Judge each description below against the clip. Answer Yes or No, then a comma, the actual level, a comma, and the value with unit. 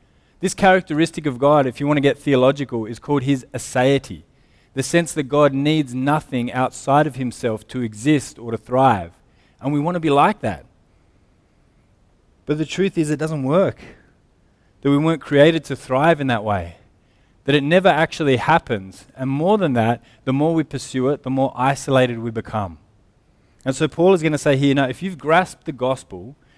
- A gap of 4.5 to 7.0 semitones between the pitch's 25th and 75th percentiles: No, average, 3.5 semitones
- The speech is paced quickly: No, average, 190 wpm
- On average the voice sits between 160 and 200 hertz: No, low, 135 Hz